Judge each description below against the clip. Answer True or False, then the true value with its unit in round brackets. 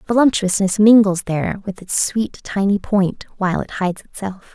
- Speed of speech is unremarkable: True (160 wpm)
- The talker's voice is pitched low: False (200 Hz)